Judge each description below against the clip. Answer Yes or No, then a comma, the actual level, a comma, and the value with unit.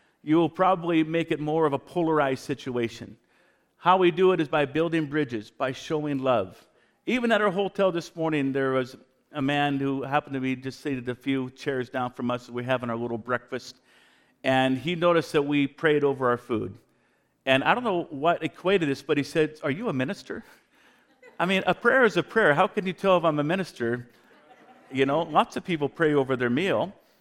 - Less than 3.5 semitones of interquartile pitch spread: No, average, 4.1 semitones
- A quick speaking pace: Yes, fast, 210 wpm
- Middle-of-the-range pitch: Yes, medium, 145 Hz